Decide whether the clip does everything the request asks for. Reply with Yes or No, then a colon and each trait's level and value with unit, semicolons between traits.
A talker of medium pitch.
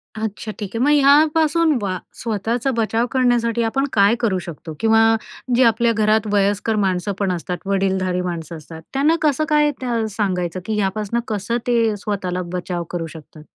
No: high, 215 Hz